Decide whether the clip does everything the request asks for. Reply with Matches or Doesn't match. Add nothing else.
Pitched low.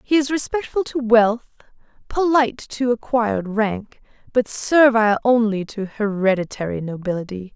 Doesn't match